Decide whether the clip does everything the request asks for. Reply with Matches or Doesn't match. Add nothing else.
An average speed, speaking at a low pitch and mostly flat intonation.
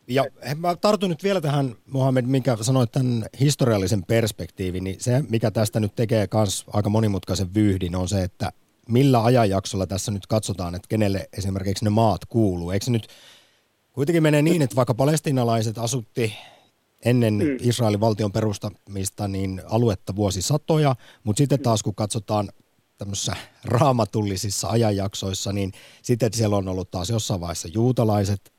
Doesn't match